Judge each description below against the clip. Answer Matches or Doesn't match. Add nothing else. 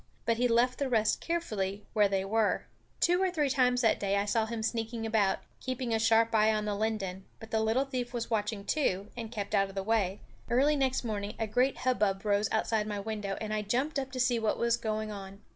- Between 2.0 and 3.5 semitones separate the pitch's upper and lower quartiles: Matches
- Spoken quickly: Matches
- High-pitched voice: Matches